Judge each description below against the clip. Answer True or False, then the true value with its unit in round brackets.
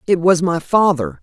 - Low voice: False (180 Hz)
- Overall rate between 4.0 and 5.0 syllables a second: True (4.6 syllables/s)